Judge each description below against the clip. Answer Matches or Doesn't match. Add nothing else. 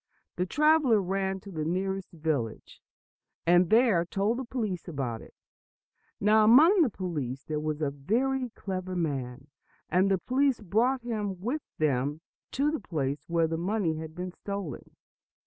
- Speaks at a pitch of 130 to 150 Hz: Doesn't match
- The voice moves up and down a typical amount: Doesn't match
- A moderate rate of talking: Matches